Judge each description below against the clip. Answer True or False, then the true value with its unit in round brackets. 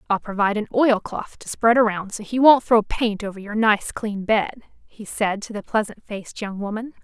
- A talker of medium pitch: False (215 Hz)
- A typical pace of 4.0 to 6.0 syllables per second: True (5.1 syllables/s)